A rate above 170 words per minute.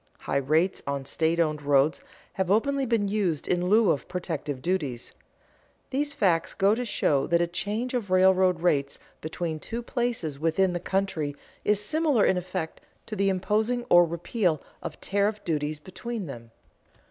No: average, 160 wpm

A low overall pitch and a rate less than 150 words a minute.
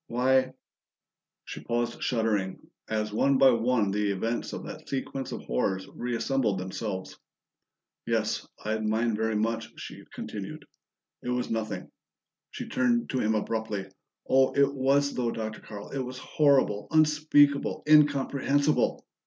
Yes: low, 120 Hz; average, 140 wpm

